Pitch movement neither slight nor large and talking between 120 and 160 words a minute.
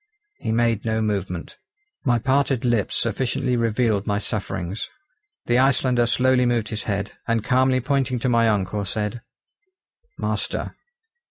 Yes: average, 3.2 semitones; slow, 135 wpm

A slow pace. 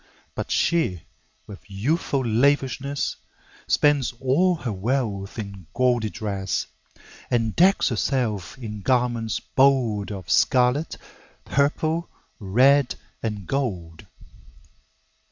Yes: slow, 95 wpm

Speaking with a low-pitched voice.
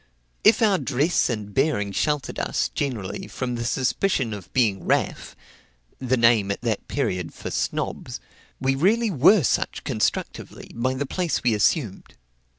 Yes: low, 130 Hz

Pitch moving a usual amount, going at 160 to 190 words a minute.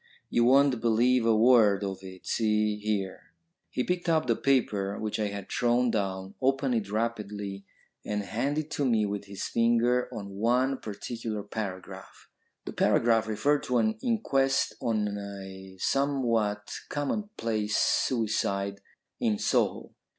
No: average, 3.7 semitones; average, 140 wpm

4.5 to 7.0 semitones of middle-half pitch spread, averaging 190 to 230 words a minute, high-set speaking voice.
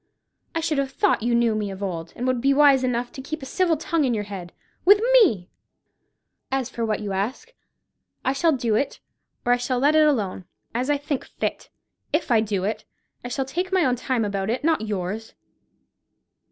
Yes: wide, 5.4 semitones; fast, 205 wpm; very high, 250 Hz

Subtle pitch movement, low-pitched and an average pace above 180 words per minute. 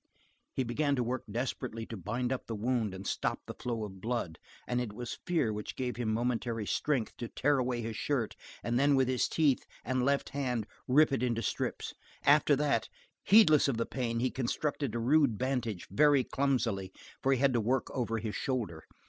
No: average, 3.1 semitones; low, 125 Hz; average, 200 wpm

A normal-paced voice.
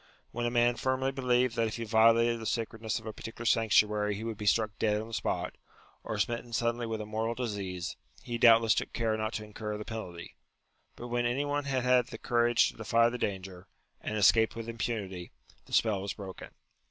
No: fast, 215 wpm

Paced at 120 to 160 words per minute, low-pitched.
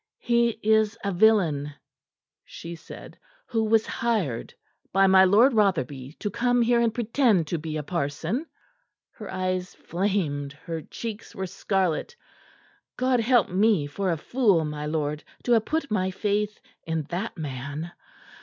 No: average, 145 wpm; high, 190 Hz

